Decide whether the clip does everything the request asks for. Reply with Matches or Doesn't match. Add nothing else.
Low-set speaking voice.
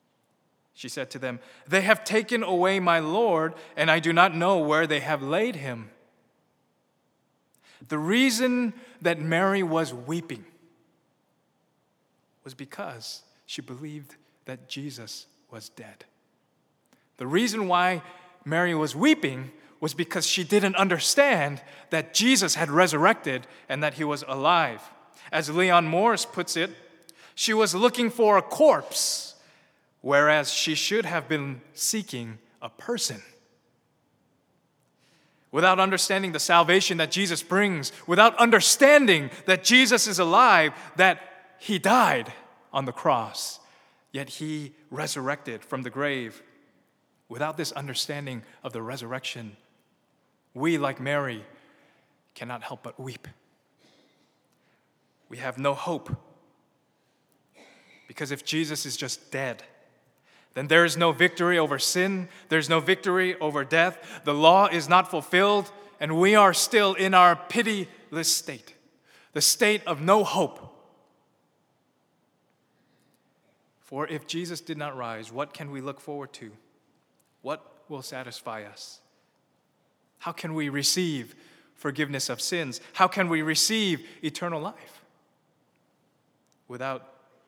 Doesn't match